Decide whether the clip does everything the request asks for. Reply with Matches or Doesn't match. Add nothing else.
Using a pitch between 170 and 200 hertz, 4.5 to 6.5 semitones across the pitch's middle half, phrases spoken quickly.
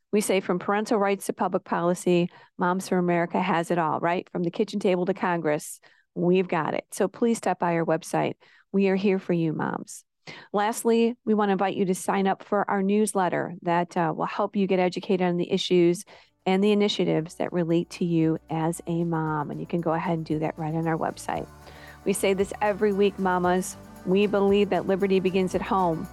Doesn't match